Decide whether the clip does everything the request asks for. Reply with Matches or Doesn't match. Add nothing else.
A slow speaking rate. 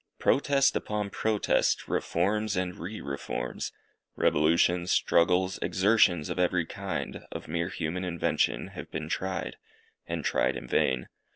Matches